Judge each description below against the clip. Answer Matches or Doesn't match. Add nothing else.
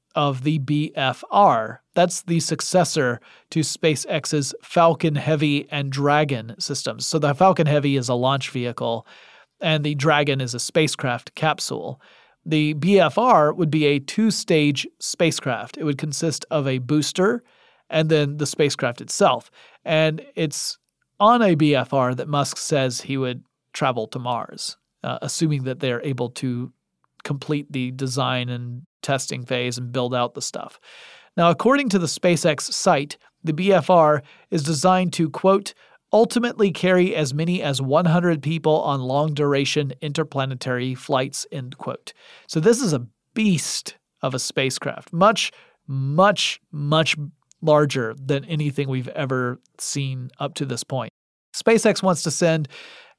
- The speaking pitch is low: Doesn't match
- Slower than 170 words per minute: Matches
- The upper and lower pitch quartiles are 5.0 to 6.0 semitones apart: Doesn't match